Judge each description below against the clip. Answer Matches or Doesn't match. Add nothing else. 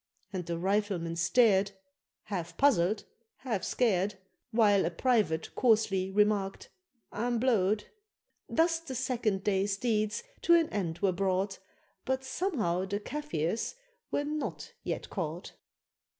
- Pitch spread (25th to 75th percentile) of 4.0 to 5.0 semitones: Matches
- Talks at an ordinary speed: Doesn't match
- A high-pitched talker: Matches